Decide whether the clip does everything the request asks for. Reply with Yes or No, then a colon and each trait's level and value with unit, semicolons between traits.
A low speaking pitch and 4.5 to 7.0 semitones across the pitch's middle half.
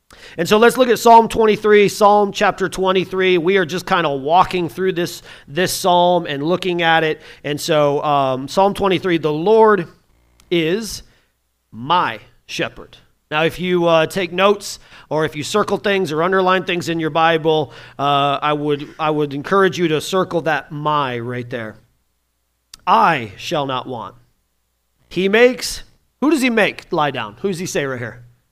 No: medium, 165 Hz; average, 5.1 semitones